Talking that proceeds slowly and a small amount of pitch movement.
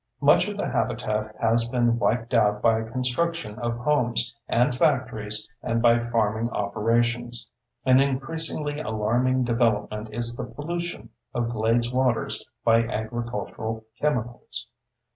Yes: slow, 125 wpm; narrow, 2.2 semitones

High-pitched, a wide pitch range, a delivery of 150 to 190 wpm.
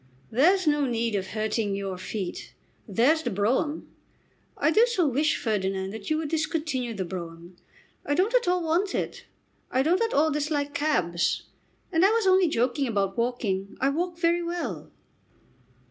Yes: very high, 280 Hz; wide, 8.3 semitones; average, 160 wpm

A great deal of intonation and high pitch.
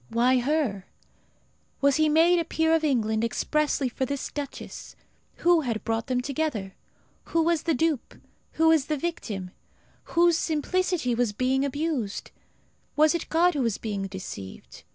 Yes: wide, 5.7 semitones; very high, 280 Hz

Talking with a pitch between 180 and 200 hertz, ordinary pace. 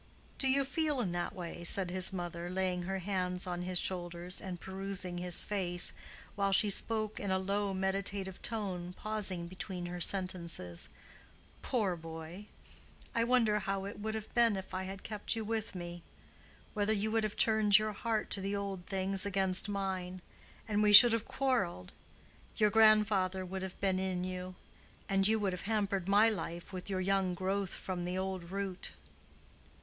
Yes: high, 190 Hz; average, 165 wpm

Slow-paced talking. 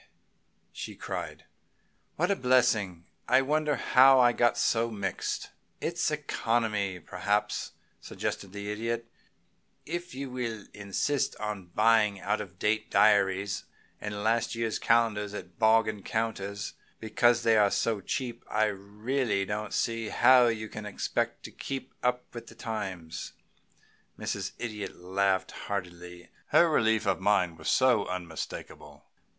Yes: slow, 130 wpm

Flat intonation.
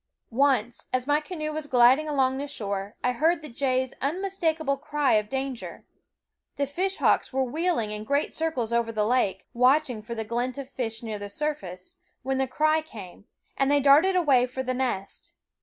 No: average, 4.1 semitones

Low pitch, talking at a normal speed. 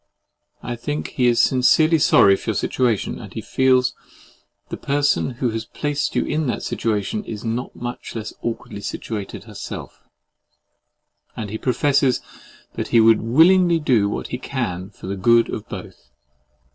Yes: low, 120 Hz; average, 165 wpm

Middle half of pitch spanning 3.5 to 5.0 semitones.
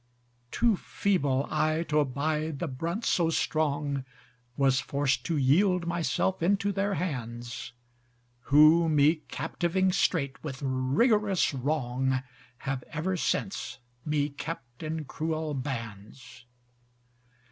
Yes: average, 4.2 semitones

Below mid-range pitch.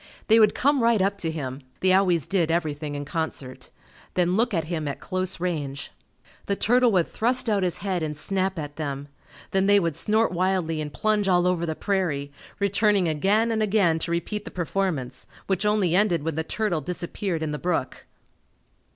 No: medium, 180 Hz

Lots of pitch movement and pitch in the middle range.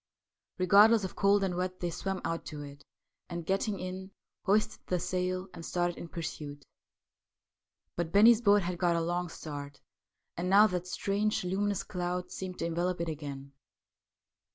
No: narrow, 2.5 semitones; medium, 180 Hz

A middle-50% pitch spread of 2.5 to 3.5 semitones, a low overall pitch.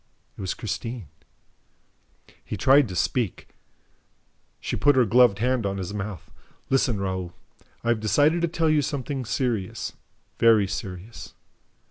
No: average, 5.0 semitones; low, 115 Hz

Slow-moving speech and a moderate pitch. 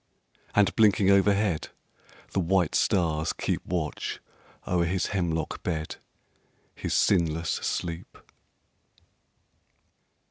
No: slow, 85 wpm; very low, 90 Hz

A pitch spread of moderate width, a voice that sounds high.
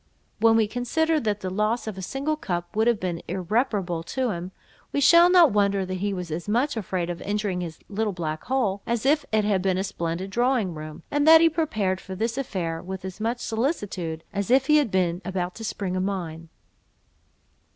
Yes: average, 4.9 semitones; high, 200 Hz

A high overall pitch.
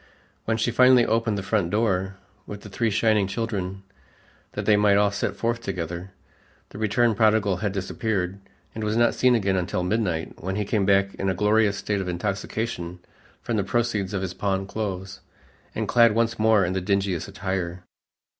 No: low, 100 Hz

